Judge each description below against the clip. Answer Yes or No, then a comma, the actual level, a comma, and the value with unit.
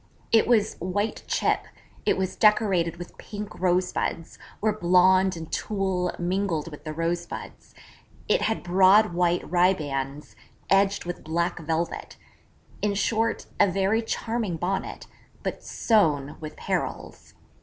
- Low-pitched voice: No, medium, 180 Hz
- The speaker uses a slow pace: Yes, slow, 125 wpm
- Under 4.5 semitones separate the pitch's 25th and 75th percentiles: Yes, average, 3.1 semitones